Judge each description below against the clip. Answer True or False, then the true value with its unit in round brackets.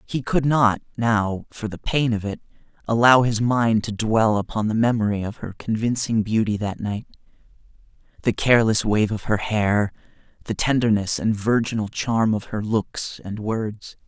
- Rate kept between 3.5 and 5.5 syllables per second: True (4.6 syllables/s)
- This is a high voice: False (110 Hz)